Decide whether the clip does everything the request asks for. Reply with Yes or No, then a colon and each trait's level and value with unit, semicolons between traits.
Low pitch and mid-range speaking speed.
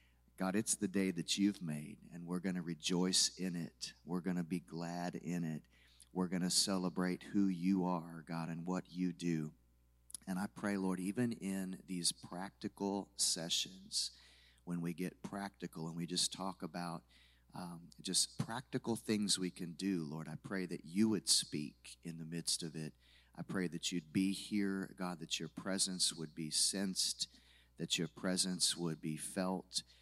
Yes: very low, 90 Hz; average, 180 wpm